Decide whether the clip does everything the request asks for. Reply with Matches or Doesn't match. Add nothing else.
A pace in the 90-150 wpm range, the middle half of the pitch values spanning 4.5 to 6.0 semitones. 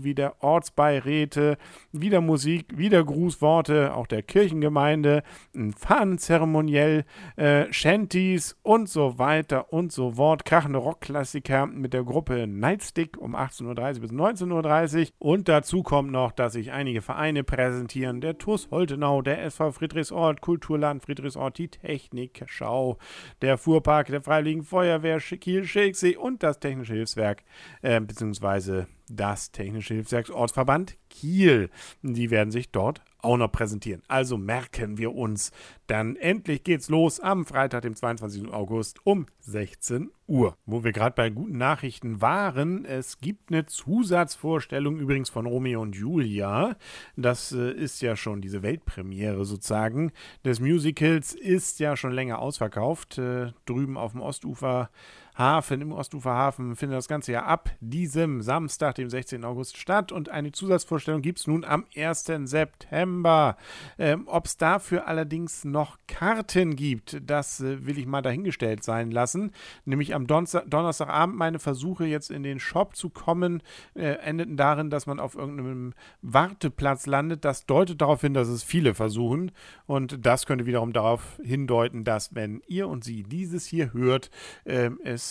Matches